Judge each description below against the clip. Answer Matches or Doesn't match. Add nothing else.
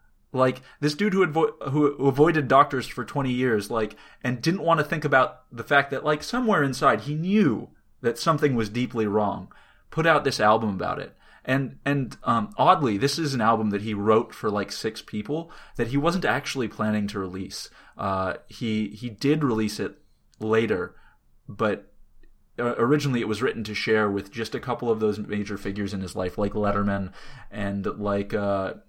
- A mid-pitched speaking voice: Doesn't match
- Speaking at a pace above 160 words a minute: Matches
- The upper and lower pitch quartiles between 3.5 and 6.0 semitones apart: Matches